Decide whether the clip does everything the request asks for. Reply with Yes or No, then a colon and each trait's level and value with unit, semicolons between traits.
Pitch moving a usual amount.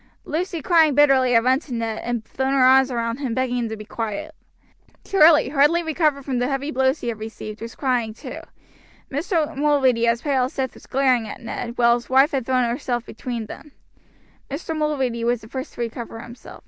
Yes: average, 3.4 semitones